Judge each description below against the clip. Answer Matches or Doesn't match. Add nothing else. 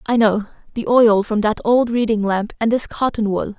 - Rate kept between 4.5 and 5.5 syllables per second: Matches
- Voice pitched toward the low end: Doesn't match